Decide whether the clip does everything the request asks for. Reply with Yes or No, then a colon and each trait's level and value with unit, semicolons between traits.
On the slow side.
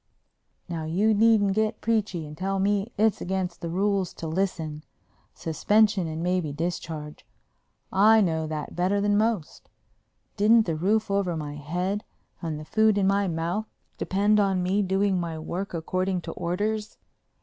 No: average, 150 wpm